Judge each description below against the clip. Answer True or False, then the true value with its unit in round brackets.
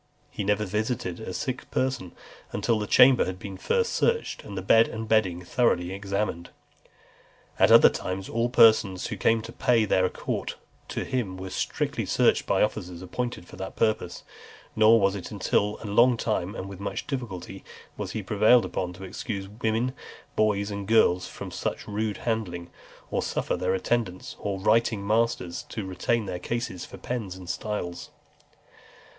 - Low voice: True (105 Hz)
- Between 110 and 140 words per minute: False (175 wpm)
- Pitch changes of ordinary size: True (3.5 semitones)